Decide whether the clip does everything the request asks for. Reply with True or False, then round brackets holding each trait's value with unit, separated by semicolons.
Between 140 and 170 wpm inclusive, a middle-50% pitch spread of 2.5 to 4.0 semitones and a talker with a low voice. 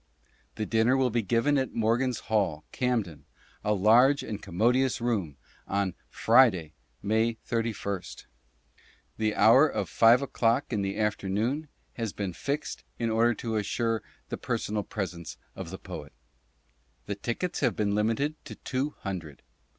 True (145 wpm; 3.5 semitones; 110 Hz)